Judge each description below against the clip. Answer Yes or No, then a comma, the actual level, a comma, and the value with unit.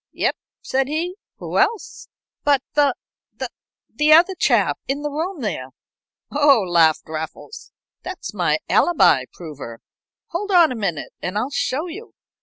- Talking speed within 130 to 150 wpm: Yes, average, 140 wpm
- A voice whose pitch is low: No, very high, 280 Hz